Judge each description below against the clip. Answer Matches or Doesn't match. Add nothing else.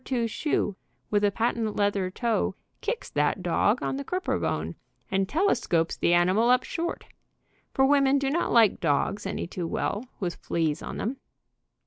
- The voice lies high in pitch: Matches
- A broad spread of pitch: Matches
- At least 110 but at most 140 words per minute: Doesn't match